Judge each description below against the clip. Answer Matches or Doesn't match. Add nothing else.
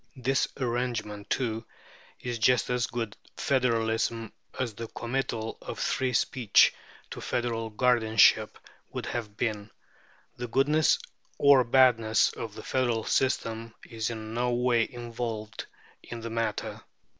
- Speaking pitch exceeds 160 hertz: Doesn't match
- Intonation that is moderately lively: Doesn't match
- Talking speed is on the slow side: Matches